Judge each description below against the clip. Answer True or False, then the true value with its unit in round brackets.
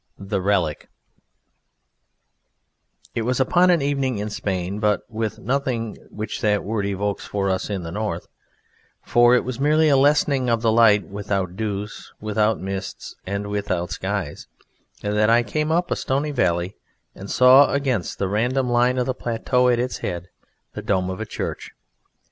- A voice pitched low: True (110 Hz)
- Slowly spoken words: False (165 wpm)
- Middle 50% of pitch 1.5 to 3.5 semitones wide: False (4.3 semitones)